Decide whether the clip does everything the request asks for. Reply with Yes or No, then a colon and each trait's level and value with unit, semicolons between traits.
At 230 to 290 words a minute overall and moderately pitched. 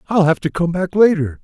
Yes: fast, 250 wpm; medium, 170 Hz